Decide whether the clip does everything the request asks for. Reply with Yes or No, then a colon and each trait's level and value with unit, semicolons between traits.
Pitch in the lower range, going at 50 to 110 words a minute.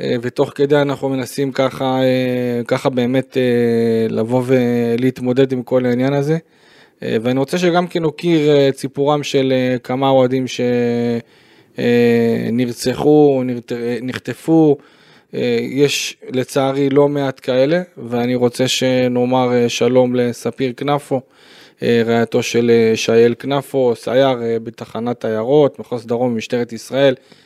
Yes: low, 130 Hz; average, 105 wpm